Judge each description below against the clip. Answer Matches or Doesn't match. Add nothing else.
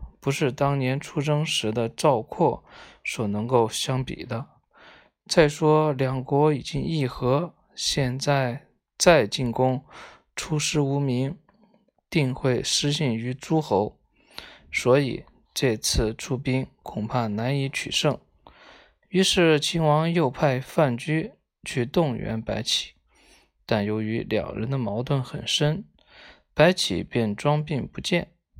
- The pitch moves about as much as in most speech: Matches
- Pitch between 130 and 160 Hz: Matches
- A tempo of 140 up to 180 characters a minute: Matches